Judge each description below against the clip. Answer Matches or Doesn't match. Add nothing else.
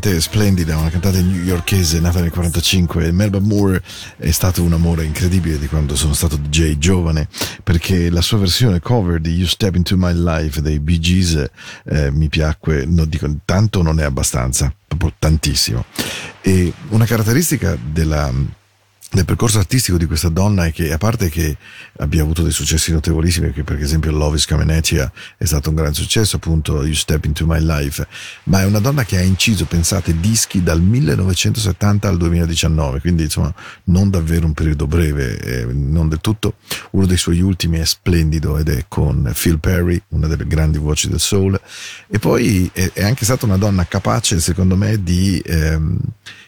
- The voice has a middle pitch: Doesn't match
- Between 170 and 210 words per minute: Matches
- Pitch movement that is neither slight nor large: Matches